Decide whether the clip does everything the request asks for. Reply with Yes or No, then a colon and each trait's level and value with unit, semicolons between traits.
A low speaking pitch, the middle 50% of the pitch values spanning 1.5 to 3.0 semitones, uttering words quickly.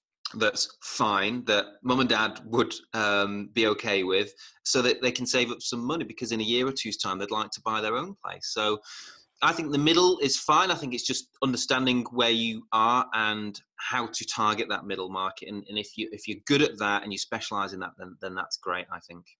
No: low, 110 Hz; average, 3.5 semitones; fast, 230 wpm